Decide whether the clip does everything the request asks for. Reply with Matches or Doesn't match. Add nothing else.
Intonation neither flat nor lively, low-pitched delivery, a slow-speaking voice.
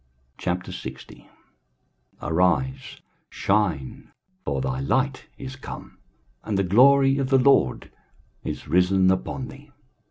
Doesn't match